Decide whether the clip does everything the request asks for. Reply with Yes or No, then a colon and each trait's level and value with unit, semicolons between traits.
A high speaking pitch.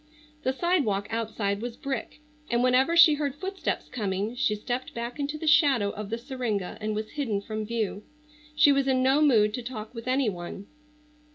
Yes: high, 245 Hz